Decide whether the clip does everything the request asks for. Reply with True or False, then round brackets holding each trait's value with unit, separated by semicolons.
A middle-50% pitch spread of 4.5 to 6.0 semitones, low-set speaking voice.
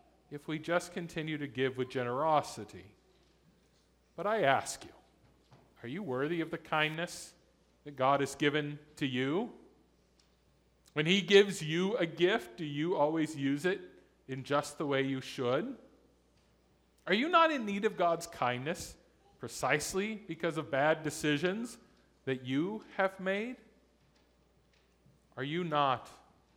False (4.8 semitones; 155 Hz)